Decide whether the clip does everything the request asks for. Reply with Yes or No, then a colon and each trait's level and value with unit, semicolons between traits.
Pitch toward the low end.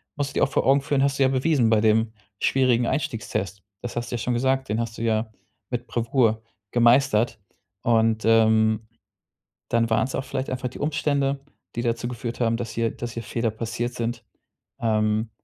Yes: low, 120 Hz